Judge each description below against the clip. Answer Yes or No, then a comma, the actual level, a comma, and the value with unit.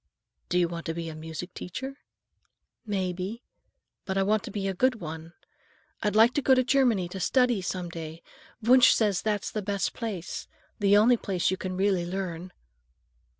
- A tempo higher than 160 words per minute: Yes, average, 175 wpm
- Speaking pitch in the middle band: No, high, 195 Hz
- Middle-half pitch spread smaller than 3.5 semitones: No, average, 3.9 semitones